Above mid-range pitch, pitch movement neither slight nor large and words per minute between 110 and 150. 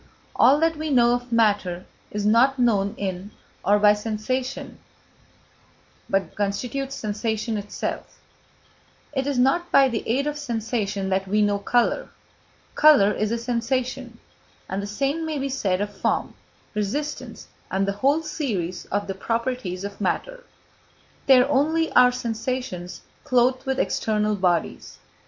Yes: high, 230 Hz; average, 4.7 semitones; average, 140 wpm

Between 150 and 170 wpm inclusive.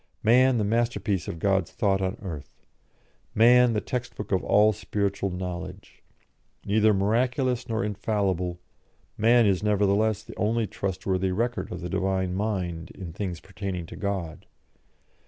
No: average, 140 wpm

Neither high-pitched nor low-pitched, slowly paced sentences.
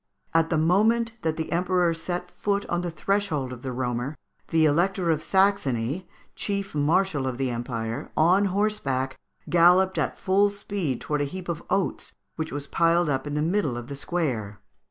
No: medium, 165 Hz; average, 175 wpm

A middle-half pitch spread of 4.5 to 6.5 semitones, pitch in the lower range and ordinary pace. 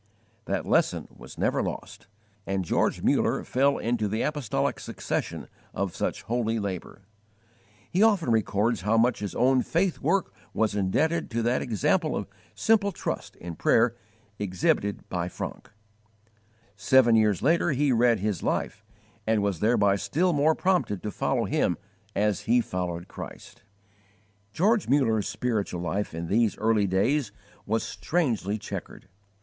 Yes: average, 5.1 semitones; low, 110 Hz; average, 145 wpm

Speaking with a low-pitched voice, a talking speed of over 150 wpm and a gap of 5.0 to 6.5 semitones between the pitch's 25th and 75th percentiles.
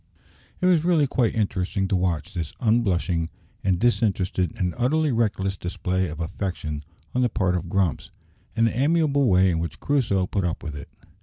Yes: very low, 95 Hz; average, 175 wpm; average, 5.3 semitones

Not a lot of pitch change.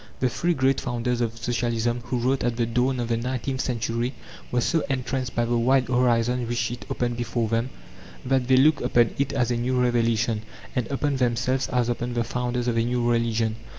Yes: narrow, 1.5 semitones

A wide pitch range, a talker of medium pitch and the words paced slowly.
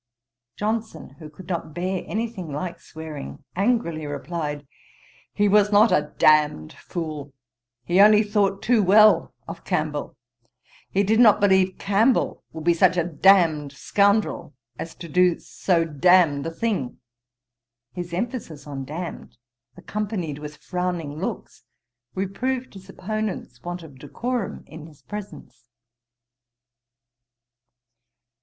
No: average, 5.0 semitones; medium, 180 Hz; slow, 125 wpm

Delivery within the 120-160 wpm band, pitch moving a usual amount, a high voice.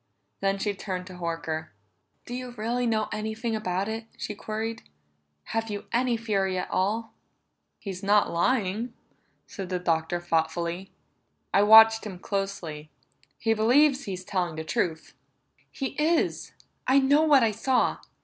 Yes: average, 145 wpm; average, 3.9 semitones; high, 210 Hz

